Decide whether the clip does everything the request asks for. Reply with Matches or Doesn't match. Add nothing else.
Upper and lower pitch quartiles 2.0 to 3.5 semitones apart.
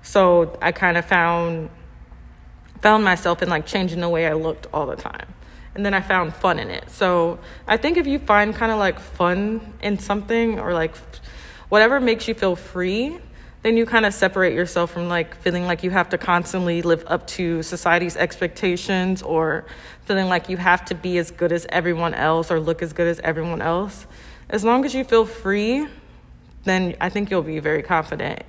Matches